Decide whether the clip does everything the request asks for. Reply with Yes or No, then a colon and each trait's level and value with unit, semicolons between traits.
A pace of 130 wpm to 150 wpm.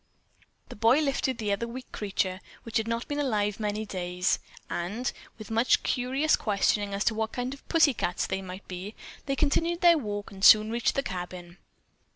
No: average, 190 wpm